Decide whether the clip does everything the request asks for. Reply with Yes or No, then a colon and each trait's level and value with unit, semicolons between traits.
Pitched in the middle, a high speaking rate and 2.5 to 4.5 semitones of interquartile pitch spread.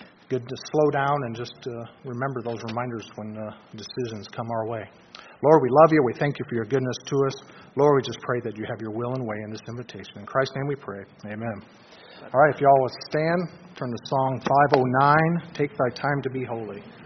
No: low, 125 Hz; fast, 230 wpm; average, 3.2 semitones